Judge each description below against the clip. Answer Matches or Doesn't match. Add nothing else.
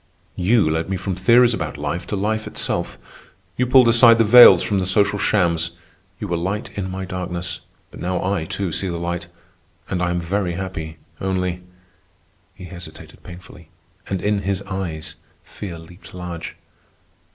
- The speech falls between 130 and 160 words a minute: Doesn't match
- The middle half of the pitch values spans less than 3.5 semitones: Matches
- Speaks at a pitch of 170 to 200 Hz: Doesn't match